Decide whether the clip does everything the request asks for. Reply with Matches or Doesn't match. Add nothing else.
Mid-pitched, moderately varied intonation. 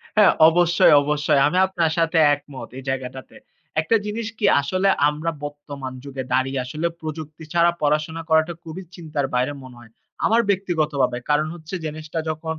Matches